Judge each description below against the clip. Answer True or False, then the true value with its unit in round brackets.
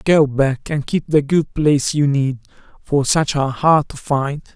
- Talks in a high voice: False (145 Hz)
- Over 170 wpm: True (200 wpm)